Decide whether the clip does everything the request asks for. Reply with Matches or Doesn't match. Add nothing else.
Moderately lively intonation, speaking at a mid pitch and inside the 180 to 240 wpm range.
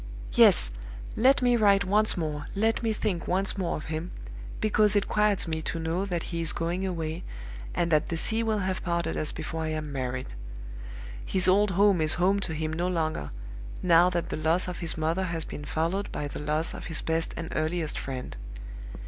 Matches